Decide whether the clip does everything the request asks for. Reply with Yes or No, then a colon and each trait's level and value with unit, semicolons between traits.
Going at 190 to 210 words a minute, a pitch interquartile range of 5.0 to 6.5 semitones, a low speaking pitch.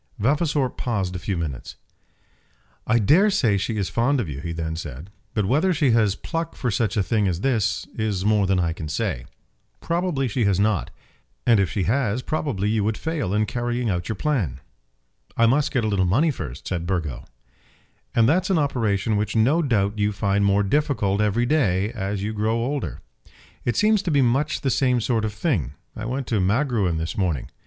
Yes: average, 200 wpm; average, 5.3 semitones; low, 110 Hz